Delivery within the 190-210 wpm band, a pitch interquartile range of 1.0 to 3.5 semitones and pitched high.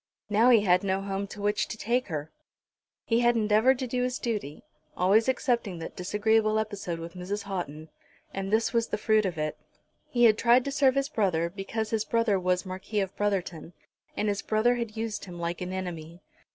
No: average, 200 wpm; average, 3.9 semitones; high, 205 Hz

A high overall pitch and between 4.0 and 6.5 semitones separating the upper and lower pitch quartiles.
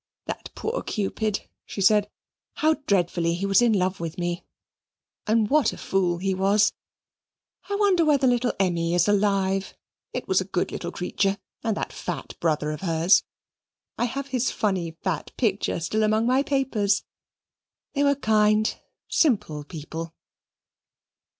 Yes: high, 200 Hz; average, 4.6 semitones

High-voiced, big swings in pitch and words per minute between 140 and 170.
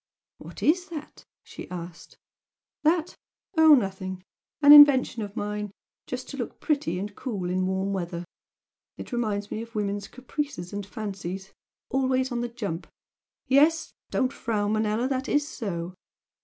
Yes: high, 220 Hz; wide, 5.8 semitones; average, 145 wpm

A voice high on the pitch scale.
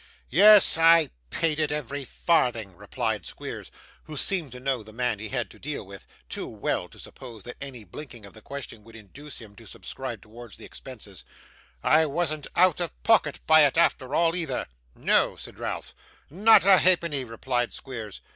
No: medium, 140 Hz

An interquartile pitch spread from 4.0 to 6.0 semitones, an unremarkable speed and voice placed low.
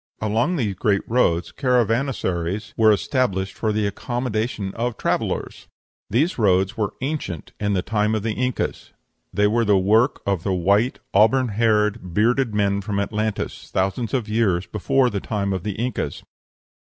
No: average, 3.1 semitones; average, 155 wpm; low, 105 Hz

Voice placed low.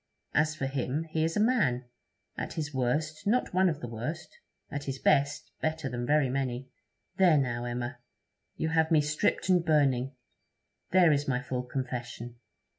No: medium, 145 Hz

